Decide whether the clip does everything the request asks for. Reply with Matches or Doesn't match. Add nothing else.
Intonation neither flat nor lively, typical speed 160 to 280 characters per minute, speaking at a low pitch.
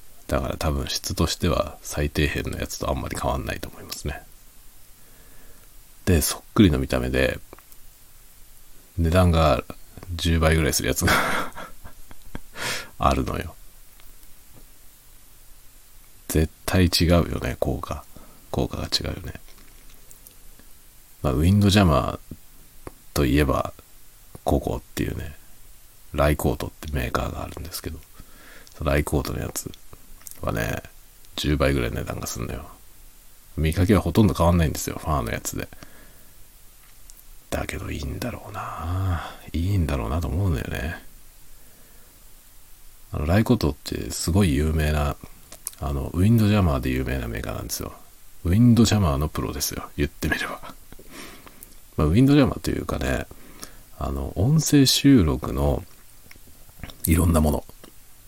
Matches